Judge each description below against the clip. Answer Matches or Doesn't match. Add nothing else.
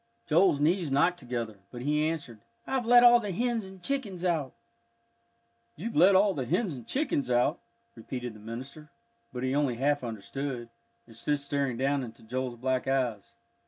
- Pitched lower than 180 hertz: Matches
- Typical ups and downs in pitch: Doesn't match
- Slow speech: Doesn't match